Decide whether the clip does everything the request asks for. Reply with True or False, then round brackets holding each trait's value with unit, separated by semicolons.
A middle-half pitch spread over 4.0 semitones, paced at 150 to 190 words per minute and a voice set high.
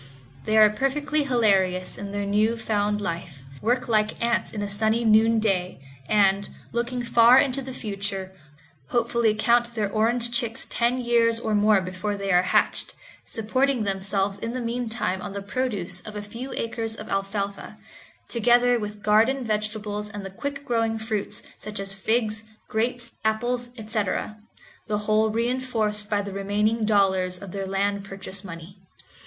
False (2.8 semitones; 155 wpm; 215 Hz)